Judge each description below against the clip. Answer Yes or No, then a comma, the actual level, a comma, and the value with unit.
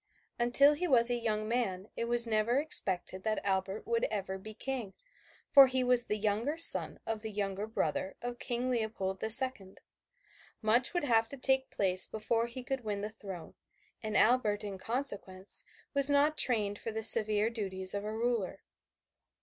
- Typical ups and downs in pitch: Yes, average, 3.6 semitones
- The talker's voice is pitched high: Yes, high, 220 Hz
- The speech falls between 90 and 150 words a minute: No, average, 175 wpm